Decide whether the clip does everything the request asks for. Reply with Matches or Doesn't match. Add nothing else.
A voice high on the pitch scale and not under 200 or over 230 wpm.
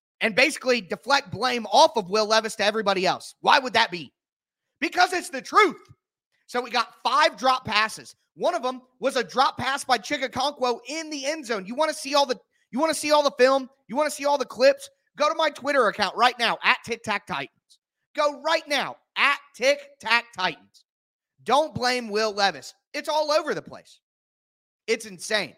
Matches